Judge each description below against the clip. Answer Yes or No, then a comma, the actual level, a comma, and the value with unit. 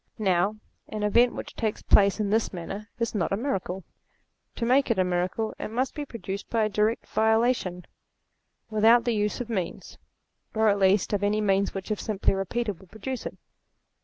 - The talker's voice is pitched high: Yes, high, 210 Hz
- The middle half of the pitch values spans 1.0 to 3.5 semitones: Yes, average, 2.9 semitones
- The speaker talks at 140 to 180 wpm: No, average, 190 wpm